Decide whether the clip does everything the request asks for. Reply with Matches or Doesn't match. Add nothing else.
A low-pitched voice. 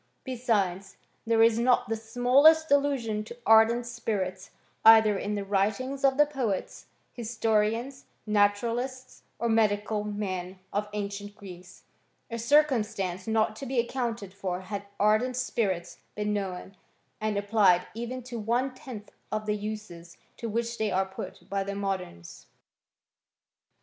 Doesn't match